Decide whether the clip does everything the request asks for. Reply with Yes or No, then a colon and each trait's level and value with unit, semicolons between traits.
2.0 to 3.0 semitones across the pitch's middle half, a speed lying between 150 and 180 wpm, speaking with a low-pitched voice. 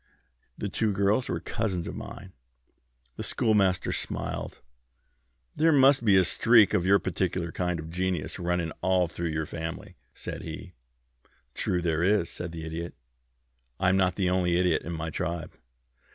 Yes: average, 2.7 semitones; average, 160 wpm; very low, 90 Hz